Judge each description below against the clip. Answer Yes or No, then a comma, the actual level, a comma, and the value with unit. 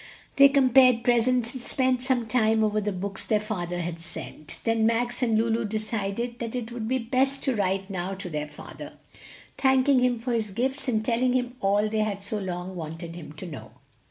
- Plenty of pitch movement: No, average, 4.2 semitones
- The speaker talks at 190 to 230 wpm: Yes, average, 200 wpm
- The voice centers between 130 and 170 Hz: No, high, 225 Hz